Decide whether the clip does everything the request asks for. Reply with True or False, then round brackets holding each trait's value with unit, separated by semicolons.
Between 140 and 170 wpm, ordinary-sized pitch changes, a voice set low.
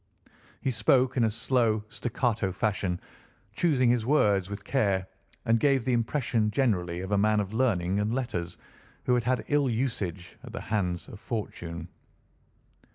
True (160 wpm; 4.3 semitones; 110 Hz)